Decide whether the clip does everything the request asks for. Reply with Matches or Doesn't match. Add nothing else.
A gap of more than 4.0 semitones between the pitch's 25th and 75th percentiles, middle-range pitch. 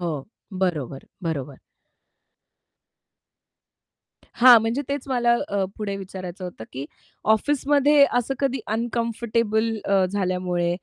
Doesn't match